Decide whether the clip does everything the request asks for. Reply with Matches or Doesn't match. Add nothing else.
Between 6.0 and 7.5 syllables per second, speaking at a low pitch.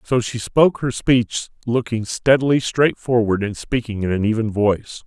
Doesn't match